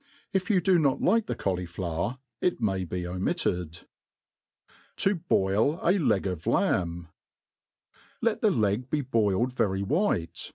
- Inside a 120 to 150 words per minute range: Yes, average, 140 wpm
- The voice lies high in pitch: No, low, 105 Hz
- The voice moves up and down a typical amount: No, wide, 9.0 semitones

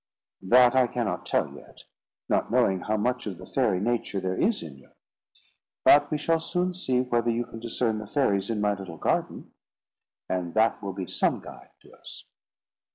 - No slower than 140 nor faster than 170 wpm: No, average, 185 wpm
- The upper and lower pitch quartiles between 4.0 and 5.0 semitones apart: Yes, average, 4.5 semitones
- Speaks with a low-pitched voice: Yes, low, 115 Hz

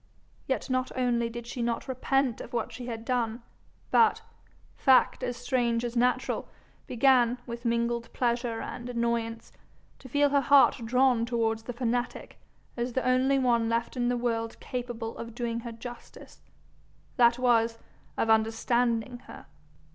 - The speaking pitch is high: Yes, high, 240 Hz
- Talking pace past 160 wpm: No, average, 155 wpm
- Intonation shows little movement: Yes, narrow, 1.3 semitones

